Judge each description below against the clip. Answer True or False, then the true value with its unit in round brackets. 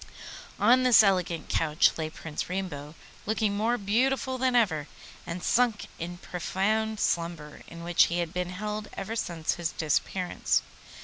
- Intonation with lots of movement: False (4.6 semitones)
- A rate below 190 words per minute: True (145 wpm)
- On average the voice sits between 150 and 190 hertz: True (185 Hz)